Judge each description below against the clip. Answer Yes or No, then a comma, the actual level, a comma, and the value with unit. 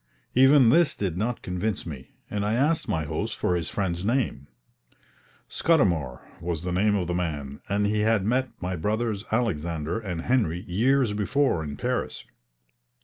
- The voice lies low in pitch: Yes, low, 100 Hz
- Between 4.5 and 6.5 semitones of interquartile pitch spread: Yes, average, 5.2 semitones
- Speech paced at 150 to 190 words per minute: Yes, average, 160 wpm